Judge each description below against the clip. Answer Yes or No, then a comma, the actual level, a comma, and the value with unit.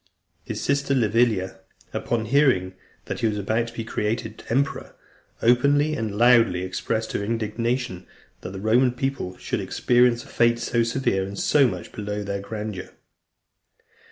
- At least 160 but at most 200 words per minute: No, average, 150 wpm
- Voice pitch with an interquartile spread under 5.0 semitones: Yes, average, 3.3 semitones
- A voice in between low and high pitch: No, low, 115 Hz